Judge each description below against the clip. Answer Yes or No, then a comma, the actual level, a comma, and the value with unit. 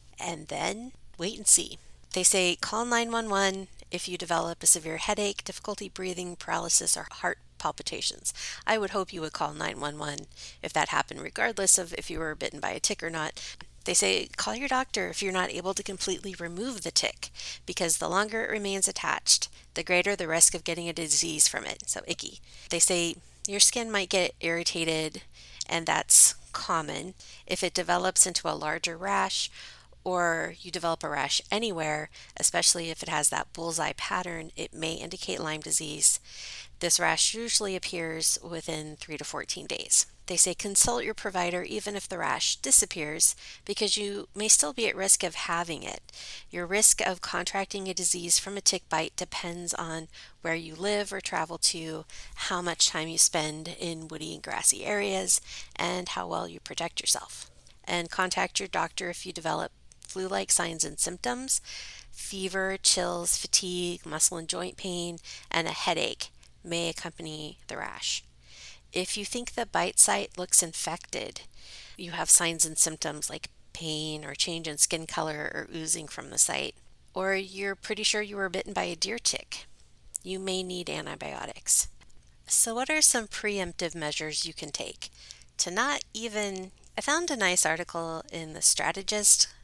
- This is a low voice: No, medium, 175 Hz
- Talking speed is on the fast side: No, average, 170 wpm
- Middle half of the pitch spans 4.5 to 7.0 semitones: No, average, 3.3 semitones